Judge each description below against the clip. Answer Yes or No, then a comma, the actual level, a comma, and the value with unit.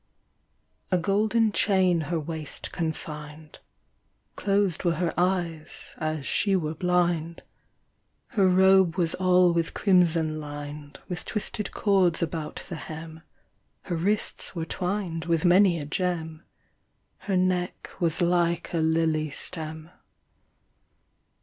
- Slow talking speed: Yes, slow, 120 wpm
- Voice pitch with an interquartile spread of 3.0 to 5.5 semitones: No, narrow, 2.5 semitones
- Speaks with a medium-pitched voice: Yes, medium, 170 Hz